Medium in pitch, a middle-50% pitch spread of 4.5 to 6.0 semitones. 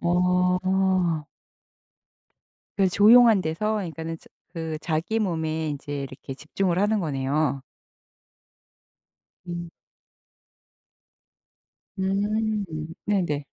No: medium, 175 Hz; average, 3.8 semitones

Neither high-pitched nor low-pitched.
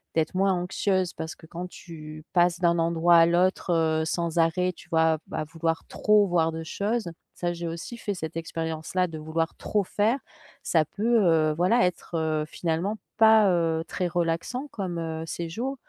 Yes: medium, 170 Hz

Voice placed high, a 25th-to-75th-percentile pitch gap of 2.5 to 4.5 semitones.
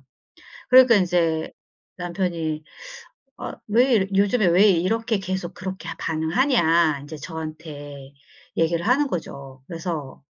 No: medium, 170 Hz; average, 3.8 semitones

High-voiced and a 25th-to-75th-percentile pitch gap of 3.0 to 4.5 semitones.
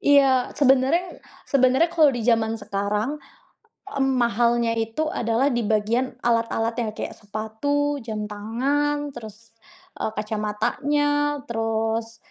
Yes: high, 235 Hz; average, 3.9 semitones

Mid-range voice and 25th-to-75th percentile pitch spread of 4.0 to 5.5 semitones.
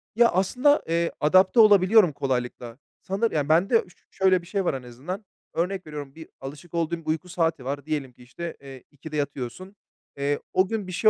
Yes: medium, 165 Hz; average, 4.8 semitones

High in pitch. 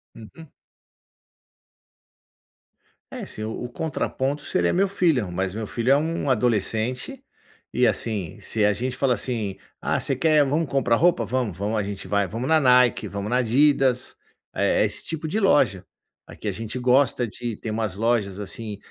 No: low, 120 Hz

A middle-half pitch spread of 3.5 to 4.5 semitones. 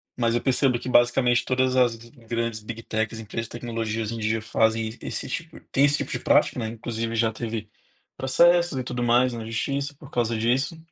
No: narrow, 2.4 semitones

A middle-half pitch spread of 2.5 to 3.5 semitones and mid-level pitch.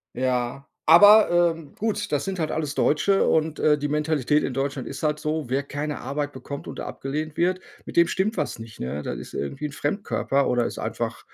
Yes: average, 2.8 semitones; medium, 150 Hz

